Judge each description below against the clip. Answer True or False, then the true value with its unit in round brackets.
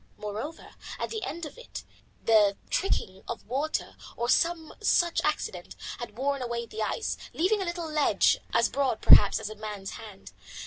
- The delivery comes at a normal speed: True (170 wpm)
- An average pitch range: False (7.2 semitones)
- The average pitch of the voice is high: True (250 Hz)